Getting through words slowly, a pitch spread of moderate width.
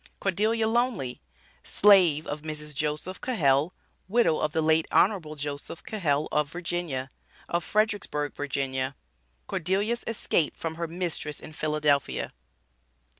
Yes: slow, 120 wpm; average, 4.6 semitones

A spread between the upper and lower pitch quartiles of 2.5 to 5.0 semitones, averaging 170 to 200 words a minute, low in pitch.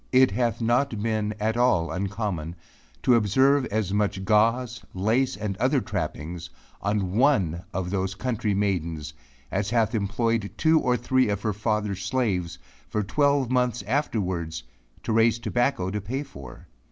No: average, 4.2 semitones; average, 150 wpm; low, 105 Hz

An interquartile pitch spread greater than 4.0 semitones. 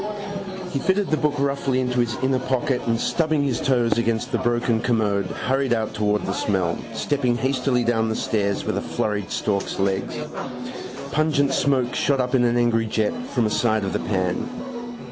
No: average, 3.6 semitones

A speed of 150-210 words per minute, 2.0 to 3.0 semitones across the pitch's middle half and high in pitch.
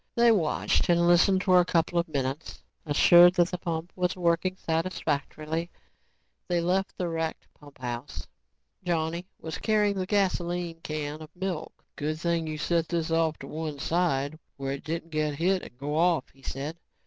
No: average, 170 wpm; narrow, 2.5 semitones; medium, 165 Hz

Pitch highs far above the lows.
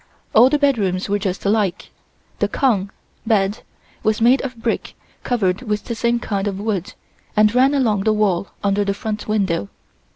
No: average, 3.0 semitones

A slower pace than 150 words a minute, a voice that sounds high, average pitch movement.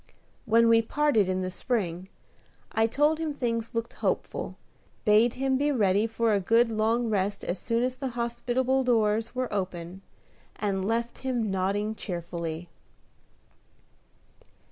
Yes: average, 140 wpm; high, 225 Hz; average, 3.7 semitones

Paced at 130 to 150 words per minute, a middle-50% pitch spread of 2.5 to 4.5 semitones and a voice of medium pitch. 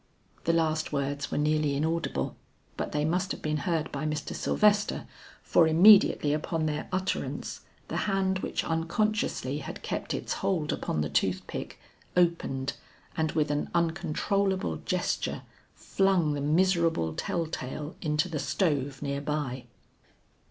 Yes: average, 140 wpm; average, 3.2 semitones; medium, 155 Hz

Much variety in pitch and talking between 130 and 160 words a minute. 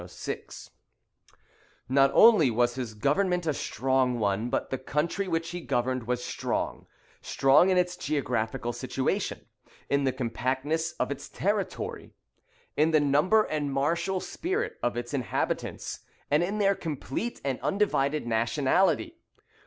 Yes: wide, 5.9 semitones; slow, 135 wpm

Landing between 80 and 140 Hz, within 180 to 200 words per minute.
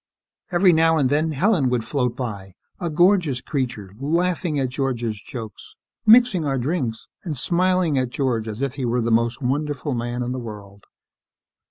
No: low, 135 Hz; average, 170 wpm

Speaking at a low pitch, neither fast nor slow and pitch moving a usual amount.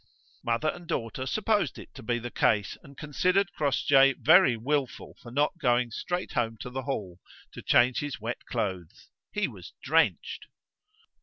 Yes: low, 130 Hz; average, 160 wpm; average, 4.2 semitones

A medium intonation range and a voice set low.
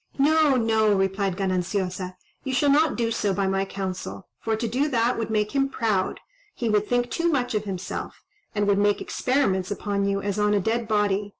No: average, 3.7 semitones; high, 210 Hz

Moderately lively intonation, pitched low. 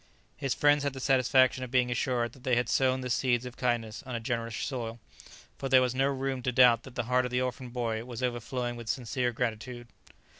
No: narrow, 1.5 semitones; low, 125 Hz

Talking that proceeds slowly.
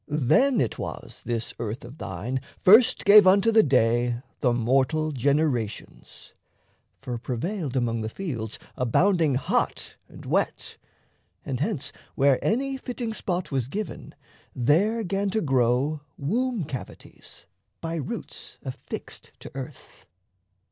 Yes: slow, 125 wpm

